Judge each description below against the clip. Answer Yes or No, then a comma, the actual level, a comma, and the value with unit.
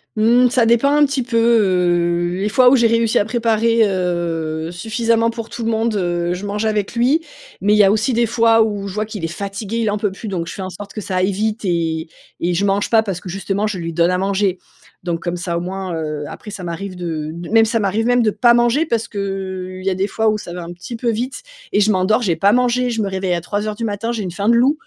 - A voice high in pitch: Yes, high, 205 Hz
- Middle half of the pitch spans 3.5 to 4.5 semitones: Yes, average, 4.1 semitones